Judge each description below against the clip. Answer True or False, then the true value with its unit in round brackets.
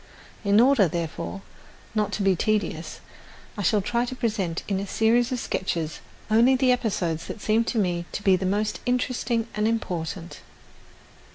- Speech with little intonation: False (3.9 semitones)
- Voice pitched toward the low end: False (210 Hz)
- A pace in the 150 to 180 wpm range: True (165 wpm)